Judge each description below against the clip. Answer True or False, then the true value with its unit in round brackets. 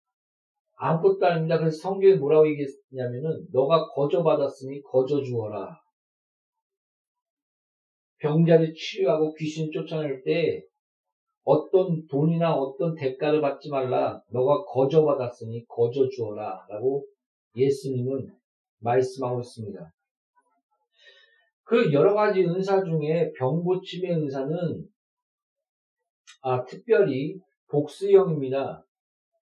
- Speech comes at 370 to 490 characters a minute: False (235 characters per minute)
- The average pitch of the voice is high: False (160 Hz)